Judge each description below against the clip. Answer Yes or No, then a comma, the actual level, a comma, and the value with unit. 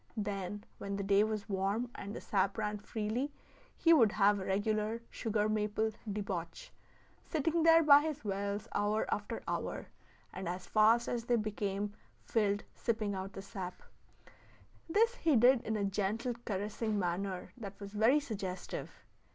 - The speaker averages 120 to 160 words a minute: Yes, average, 155 wpm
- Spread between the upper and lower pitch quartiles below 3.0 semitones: Yes, narrow, 2.6 semitones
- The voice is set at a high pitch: Yes, high, 210 Hz